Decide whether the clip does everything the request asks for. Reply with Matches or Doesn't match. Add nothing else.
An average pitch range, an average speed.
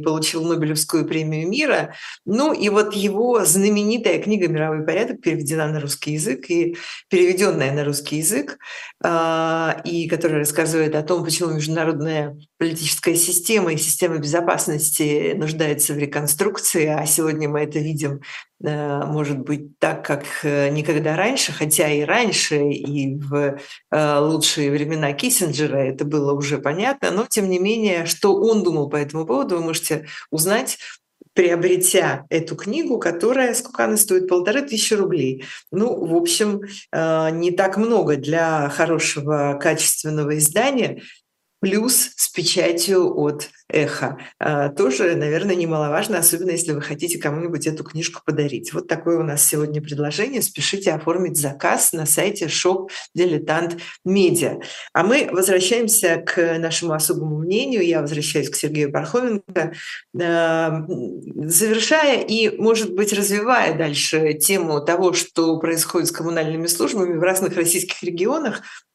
Matches